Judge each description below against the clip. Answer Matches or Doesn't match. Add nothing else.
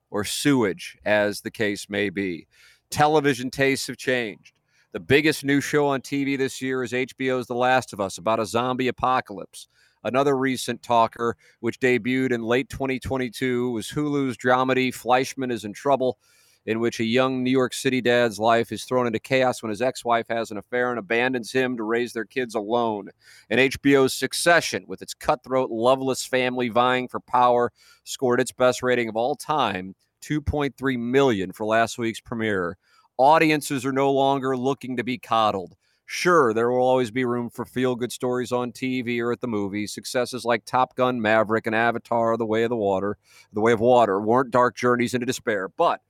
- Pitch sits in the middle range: Doesn't match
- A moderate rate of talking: Matches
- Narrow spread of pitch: Matches